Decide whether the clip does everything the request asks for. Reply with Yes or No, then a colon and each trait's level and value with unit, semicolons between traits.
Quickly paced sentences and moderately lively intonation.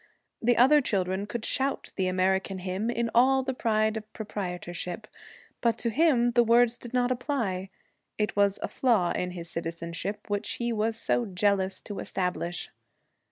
No: average, 160 wpm; average, 4.3 semitones